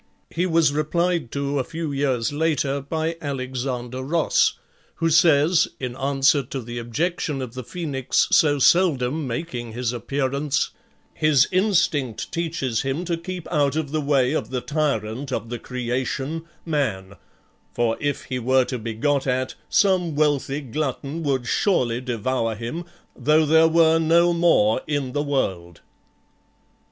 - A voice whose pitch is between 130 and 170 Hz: Yes, medium, 140 Hz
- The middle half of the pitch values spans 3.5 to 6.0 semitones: Yes, average, 4.0 semitones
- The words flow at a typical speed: Yes, average, 145 wpm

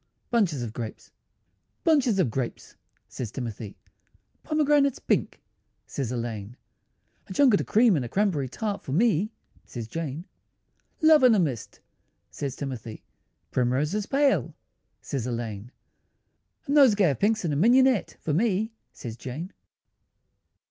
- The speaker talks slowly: Yes, slow, 130 wpm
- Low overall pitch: No, medium, 165 Hz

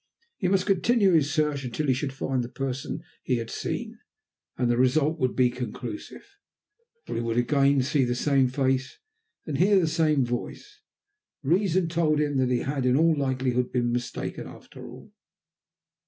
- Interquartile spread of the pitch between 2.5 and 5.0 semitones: Yes, average, 4.0 semitones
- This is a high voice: No, low, 135 Hz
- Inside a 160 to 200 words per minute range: Yes, average, 170 wpm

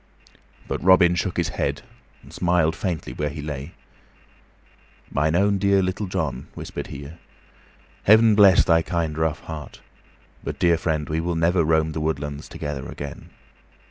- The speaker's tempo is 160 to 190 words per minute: No, average, 150 wpm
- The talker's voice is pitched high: No, very low, 80 Hz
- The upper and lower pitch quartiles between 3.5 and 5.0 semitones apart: No, average, 3.1 semitones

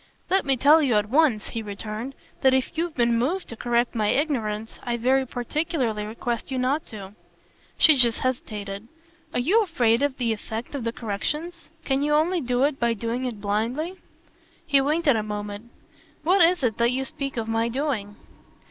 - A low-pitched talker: No, high, 245 Hz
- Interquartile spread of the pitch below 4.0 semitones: No, average, 4.4 semitones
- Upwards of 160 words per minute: Yes, average, 185 wpm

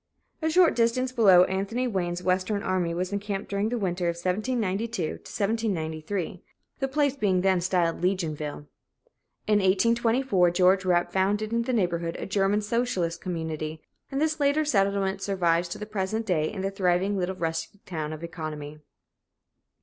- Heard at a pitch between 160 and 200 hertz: Yes, high, 190 Hz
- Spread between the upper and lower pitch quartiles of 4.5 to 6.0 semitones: No, average, 3.7 semitones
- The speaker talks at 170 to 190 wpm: No, average, 155 wpm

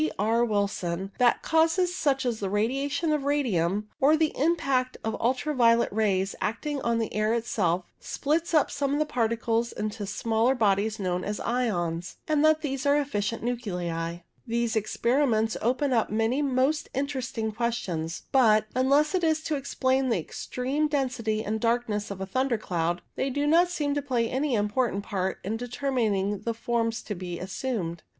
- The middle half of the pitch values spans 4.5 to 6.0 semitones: Yes, average, 4.8 semitones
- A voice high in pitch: Yes, high, 235 Hz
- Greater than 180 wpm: No, average, 170 wpm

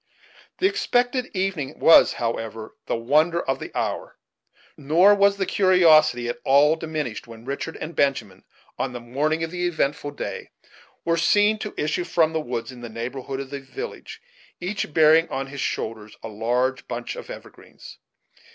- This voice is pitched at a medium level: Yes, medium, 150 Hz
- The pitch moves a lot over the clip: Yes, wide, 5.8 semitones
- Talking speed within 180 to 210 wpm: No, average, 165 wpm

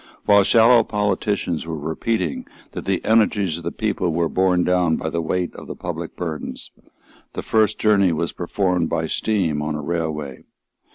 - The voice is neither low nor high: No, very low, 90 Hz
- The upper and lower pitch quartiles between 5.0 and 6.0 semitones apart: No, average, 4.1 semitones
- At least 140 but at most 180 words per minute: Yes, average, 170 wpm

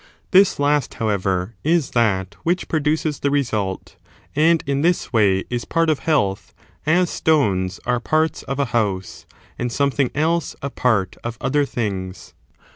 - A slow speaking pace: No, average, 155 wpm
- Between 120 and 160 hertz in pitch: Yes, low, 135 Hz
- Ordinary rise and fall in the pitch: No, wide, 7.2 semitones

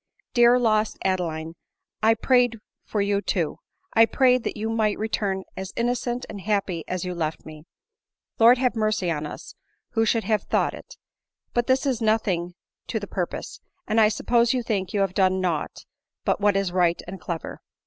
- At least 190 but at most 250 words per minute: No, average, 180 wpm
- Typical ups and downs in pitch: Yes, average, 3.8 semitones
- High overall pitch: Yes, high, 210 Hz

